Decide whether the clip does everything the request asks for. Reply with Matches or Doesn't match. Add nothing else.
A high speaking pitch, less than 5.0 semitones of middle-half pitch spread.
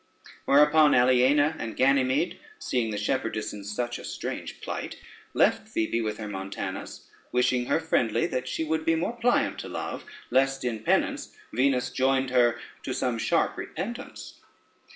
Doesn't match